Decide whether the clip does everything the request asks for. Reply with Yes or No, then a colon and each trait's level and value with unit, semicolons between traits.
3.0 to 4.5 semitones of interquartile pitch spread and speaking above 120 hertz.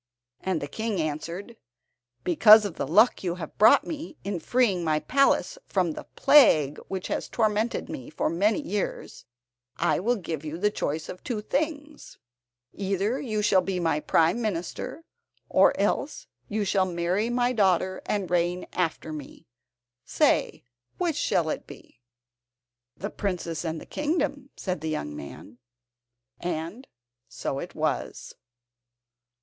No: wide, 5.4 semitones; high, 190 Hz